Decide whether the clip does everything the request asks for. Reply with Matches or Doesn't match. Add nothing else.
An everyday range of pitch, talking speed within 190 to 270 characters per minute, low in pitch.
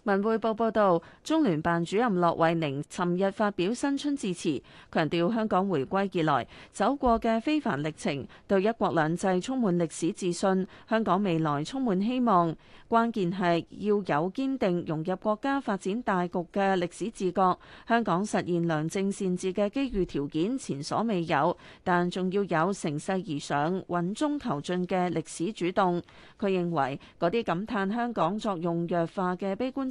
Doesn't match